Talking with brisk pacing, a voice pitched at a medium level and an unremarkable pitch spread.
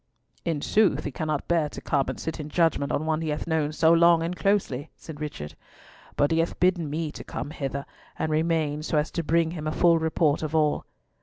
No: fast, 225 wpm; medium, 155 Hz; narrow, 1.9 semitones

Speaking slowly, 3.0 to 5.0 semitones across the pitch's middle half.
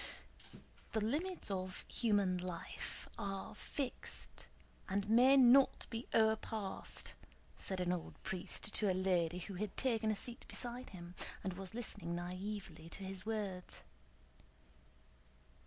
Yes: slow, 125 wpm; average, 3.5 semitones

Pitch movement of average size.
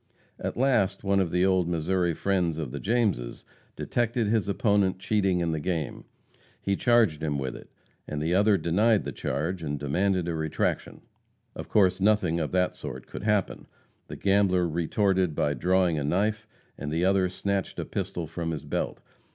Yes: average, 3.6 semitones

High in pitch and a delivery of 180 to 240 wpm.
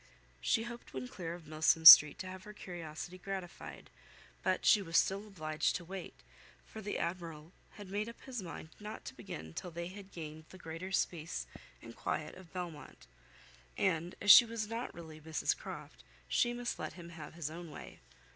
No: medium, 175 Hz; average, 185 wpm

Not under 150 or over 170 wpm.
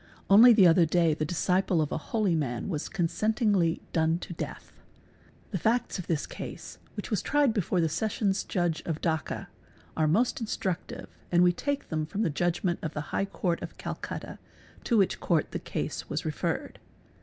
No: average, 180 wpm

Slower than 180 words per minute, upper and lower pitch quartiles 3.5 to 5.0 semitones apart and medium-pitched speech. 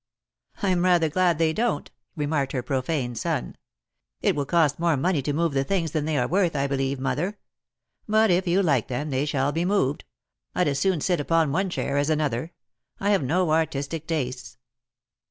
No: average, 190 wpm; average, 4.2 semitones; medium, 155 Hz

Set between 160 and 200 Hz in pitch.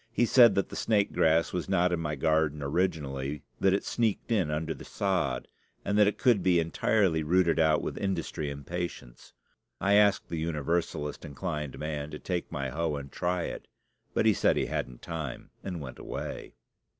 No: very low, 80 Hz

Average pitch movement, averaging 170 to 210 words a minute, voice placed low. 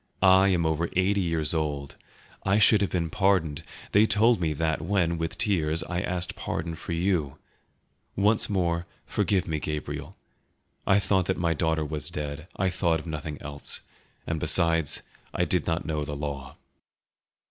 No: average, 3.4 semitones; average, 160 wpm; very low, 85 Hz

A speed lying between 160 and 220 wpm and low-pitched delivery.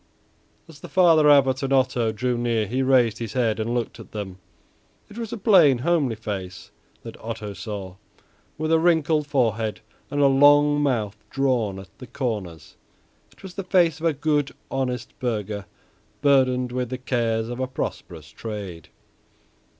Yes: average, 165 wpm; low, 125 Hz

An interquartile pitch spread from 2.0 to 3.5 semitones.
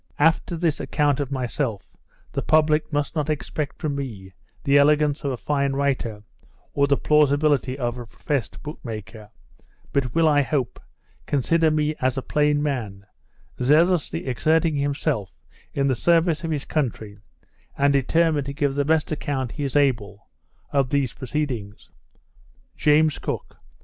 Yes: average, 2.8 semitones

